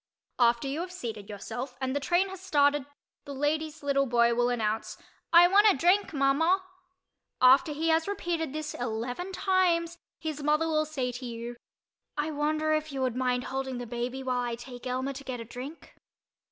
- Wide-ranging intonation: No, average, 4.5 semitones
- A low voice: No, very high, 275 Hz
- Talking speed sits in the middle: Yes, average, 185 wpm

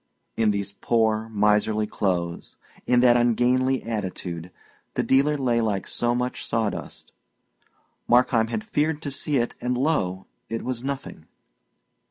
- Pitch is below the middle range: Yes, low, 120 Hz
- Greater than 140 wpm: No, slow, 135 wpm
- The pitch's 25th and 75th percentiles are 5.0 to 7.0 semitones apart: No, average, 3.4 semitones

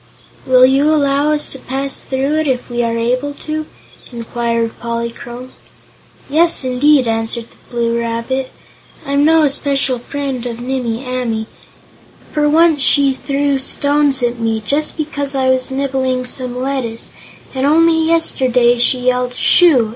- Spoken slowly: No, average, 145 wpm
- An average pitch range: Yes, average, 3.0 semitones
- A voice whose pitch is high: Yes, very high, 260 Hz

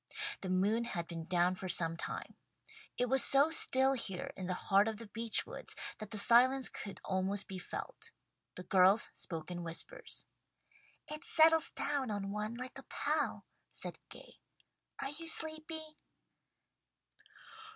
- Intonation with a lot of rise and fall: Yes, wide, 6.5 semitones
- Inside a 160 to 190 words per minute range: No, average, 150 wpm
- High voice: Yes, high, 215 Hz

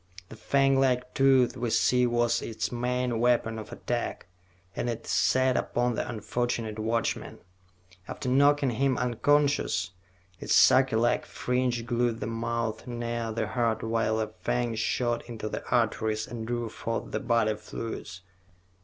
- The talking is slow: No, average, 145 wpm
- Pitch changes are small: Yes, narrow, 1.8 semitones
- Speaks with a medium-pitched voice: No, low, 120 Hz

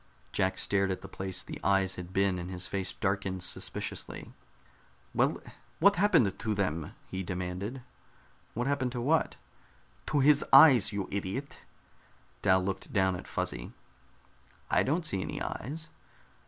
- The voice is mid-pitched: No, low, 100 Hz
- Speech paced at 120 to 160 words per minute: Yes, average, 145 wpm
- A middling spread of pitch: No, wide, 5.9 semitones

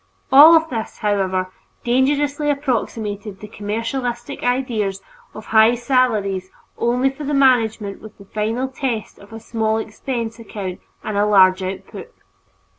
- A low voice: No, high, 225 Hz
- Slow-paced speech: Yes, slow, 130 wpm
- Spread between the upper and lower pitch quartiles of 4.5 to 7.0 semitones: No, average, 3.9 semitones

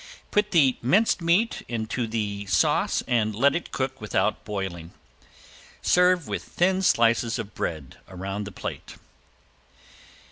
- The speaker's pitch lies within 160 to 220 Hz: No, low, 115 Hz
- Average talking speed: No, slow, 130 wpm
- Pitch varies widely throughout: Yes, wide, 8.8 semitones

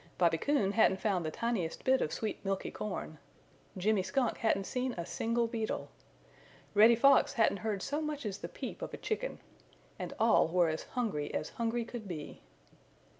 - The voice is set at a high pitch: Yes, high, 215 Hz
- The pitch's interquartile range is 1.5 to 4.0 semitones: No, average, 4.4 semitones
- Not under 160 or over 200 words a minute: Yes, average, 175 wpm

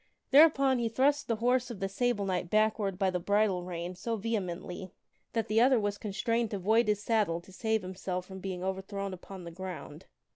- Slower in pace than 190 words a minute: No, average, 195 wpm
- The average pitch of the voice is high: Yes, high, 200 Hz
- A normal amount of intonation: Yes, average, 3.6 semitones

